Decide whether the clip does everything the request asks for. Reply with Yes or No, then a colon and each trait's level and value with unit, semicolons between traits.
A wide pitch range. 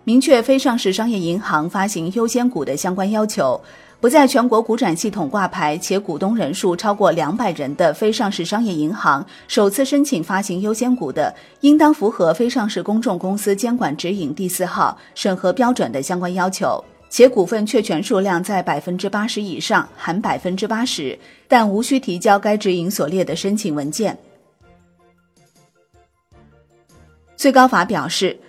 No: average, 4.6 semitones